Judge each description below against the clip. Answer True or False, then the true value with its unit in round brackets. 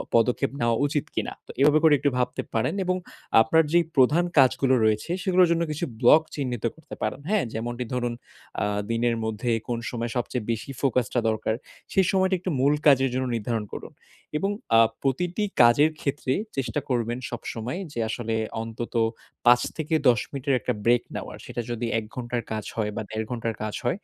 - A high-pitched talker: False (125 Hz)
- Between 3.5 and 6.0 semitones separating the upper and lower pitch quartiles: True (4.1 semitones)